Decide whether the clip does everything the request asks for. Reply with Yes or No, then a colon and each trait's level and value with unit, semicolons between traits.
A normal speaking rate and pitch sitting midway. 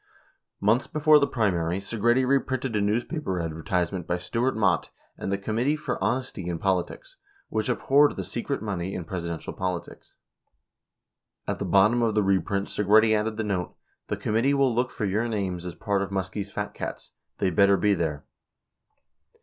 No: average, 175 wpm; low, 105 Hz